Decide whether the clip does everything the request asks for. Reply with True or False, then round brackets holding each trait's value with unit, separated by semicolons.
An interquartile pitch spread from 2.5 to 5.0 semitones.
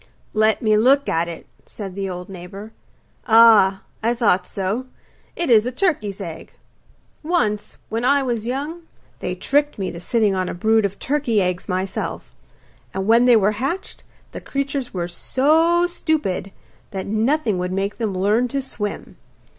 False (5.4 semitones)